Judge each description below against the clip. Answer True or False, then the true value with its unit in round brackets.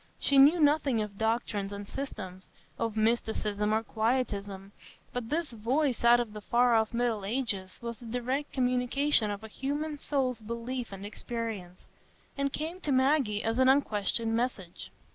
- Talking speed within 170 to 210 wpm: False (160 wpm)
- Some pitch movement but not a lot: True (3.9 semitones)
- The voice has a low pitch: False (235 Hz)